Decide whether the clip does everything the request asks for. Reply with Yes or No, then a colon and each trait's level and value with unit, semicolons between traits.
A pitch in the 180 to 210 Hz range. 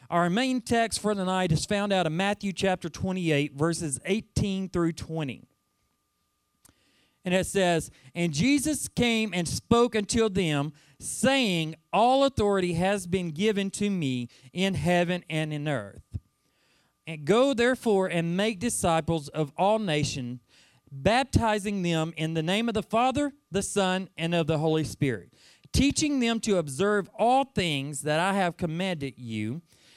Yes: medium, 185 Hz